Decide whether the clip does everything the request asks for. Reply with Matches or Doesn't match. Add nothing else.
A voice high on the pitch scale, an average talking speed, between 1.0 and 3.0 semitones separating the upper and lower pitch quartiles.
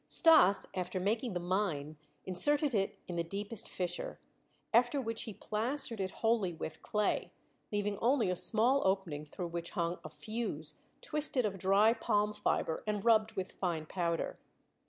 Doesn't match